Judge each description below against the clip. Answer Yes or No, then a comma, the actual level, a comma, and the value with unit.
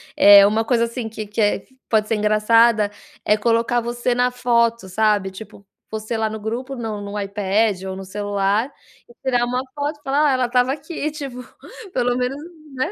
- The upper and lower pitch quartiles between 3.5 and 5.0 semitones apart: No, average, 3.0 semitones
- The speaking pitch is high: Yes, high, 230 Hz